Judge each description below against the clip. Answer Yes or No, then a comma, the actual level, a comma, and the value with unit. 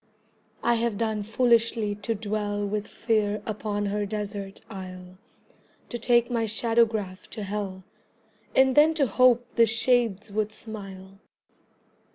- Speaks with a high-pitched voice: Yes, high, 215 Hz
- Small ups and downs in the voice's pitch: Yes, narrow, 2.3 semitones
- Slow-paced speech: Yes, slow, 130 wpm